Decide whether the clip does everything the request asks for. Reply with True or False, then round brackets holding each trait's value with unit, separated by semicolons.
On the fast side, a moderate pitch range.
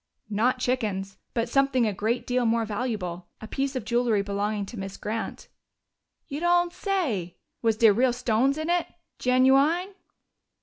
False (160 wpm; 4.3 semitones)